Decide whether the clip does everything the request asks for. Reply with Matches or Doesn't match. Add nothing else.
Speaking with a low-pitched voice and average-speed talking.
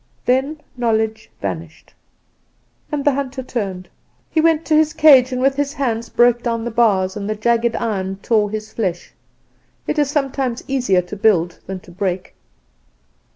Doesn't match